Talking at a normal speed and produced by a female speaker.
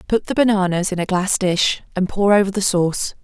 No: fast, 225 wpm; female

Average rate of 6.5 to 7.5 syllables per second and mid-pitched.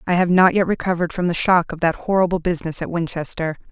Yes: 6.7 syllables/s; medium, 175 Hz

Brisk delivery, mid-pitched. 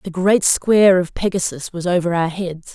No: average, 195 wpm; medium, 180 Hz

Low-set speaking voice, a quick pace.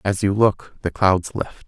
Yes: very low, 95 Hz; fast, 215 wpm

